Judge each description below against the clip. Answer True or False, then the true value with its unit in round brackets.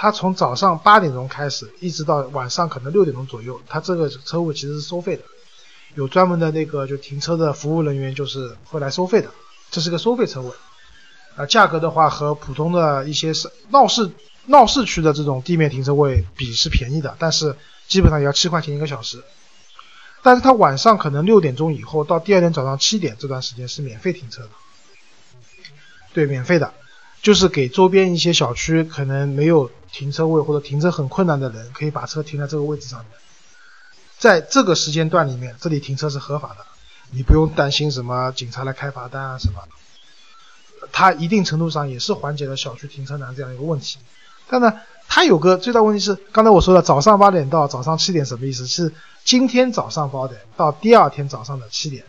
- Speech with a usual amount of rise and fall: True (4.9 semitones)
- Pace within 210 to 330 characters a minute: True (315 characters per minute)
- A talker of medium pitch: True (150 Hz)